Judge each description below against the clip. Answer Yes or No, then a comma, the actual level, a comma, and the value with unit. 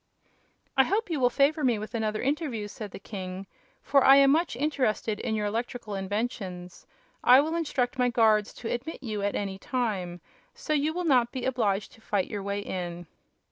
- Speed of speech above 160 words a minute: Yes, average, 190 wpm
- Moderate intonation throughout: Yes, average, 5.0 semitones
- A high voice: Yes, high, 230 Hz